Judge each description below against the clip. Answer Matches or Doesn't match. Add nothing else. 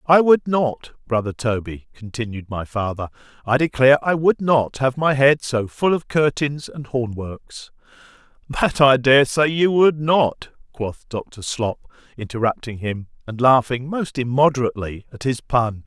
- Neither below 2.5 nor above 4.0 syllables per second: Doesn't match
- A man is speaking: Matches